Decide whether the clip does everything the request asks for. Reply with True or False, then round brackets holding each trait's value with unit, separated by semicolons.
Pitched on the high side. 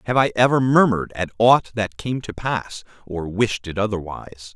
False (110 Hz)